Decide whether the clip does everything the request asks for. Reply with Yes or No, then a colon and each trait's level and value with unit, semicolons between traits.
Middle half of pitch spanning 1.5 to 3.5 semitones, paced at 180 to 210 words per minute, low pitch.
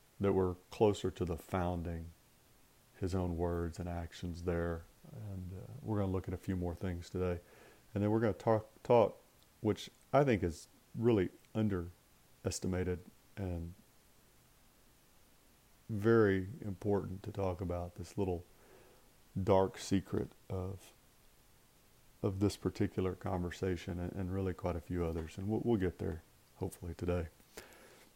No: average, 2.8 semitones; slow, 135 wpm; very low, 95 Hz